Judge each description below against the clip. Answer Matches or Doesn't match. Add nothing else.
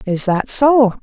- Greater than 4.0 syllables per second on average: Doesn't match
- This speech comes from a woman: Matches